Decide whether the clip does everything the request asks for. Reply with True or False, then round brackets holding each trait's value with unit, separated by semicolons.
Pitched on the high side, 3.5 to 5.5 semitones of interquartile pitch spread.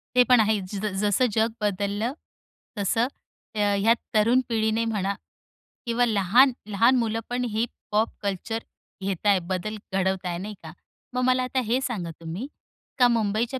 False (215 Hz; 3.1 semitones)